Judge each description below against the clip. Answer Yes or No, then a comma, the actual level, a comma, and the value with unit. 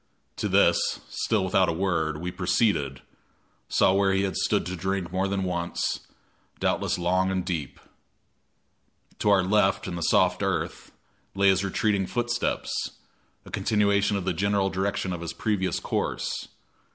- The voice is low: Yes, very low, 95 Hz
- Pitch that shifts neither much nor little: No, narrow, 1.9 semitones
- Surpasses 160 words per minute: No, average, 150 wpm